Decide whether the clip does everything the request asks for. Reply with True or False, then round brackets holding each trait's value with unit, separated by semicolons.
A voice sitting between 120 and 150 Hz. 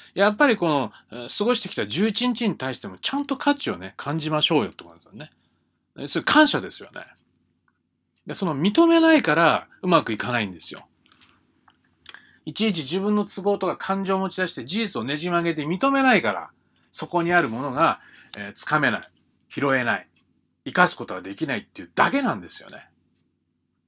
False (185 Hz)